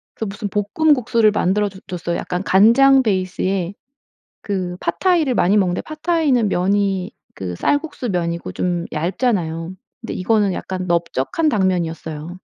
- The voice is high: Yes, high, 195 Hz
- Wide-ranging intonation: No, average, 4.4 semitones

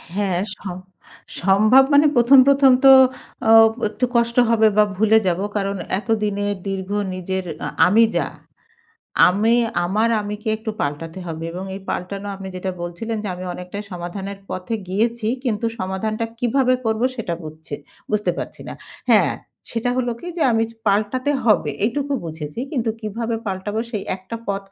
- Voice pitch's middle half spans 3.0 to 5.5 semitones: Yes, average, 3.5 semitones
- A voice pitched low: No, high, 210 Hz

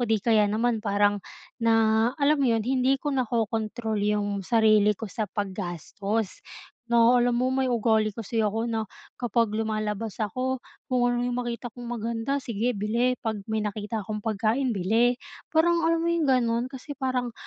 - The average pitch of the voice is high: Yes, high, 225 Hz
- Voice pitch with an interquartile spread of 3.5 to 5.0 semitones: No, average, 2.7 semitones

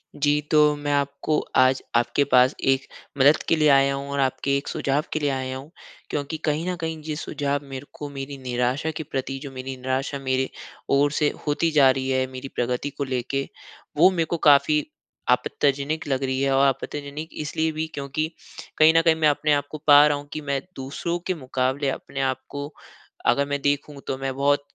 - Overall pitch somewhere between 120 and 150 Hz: Yes, medium, 140 Hz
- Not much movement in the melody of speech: Yes, narrow, 1.9 semitones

